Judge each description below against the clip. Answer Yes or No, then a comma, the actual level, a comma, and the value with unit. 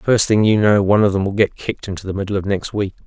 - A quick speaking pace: Yes, fast, 315 wpm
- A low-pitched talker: Yes, low, 100 Hz